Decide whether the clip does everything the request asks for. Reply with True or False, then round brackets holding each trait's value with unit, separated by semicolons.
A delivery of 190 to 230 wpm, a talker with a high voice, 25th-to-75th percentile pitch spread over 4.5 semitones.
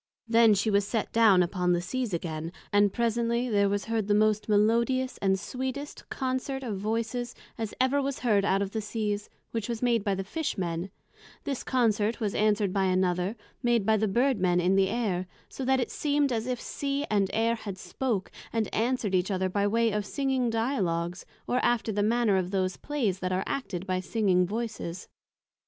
False (195 wpm; 215 Hz; 3.8 semitones)